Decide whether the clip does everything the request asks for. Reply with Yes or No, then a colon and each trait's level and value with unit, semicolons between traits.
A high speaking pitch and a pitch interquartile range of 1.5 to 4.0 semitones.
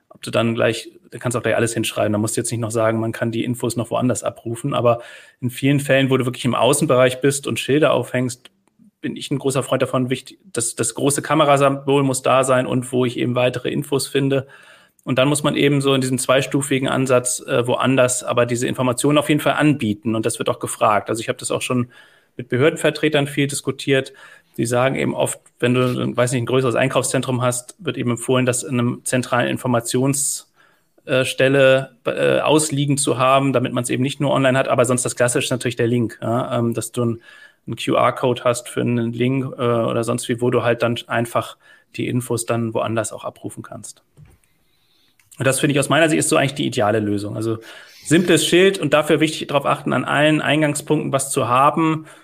No: low, 130 Hz; average, 2.7 semitones